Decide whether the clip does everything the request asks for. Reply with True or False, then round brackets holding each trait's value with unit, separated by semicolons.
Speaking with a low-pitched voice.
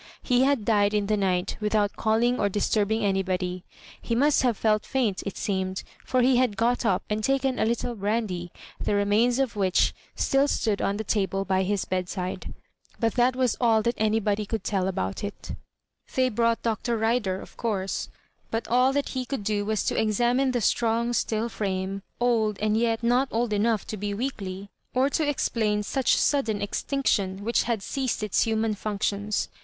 False (220 Hz)